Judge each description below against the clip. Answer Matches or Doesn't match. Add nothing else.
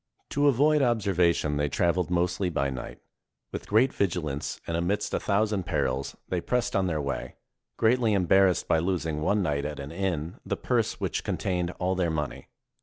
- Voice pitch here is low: Matches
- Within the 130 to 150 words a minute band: Doesn't match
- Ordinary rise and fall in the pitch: Matches